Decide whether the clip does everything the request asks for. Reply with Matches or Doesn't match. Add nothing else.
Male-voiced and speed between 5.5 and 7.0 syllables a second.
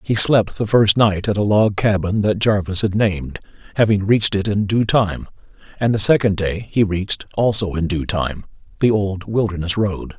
Doesn't match